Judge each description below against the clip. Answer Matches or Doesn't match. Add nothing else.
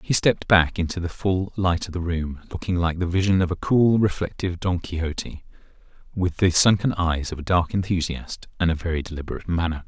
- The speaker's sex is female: Doesn't match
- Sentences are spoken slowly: Doesn't match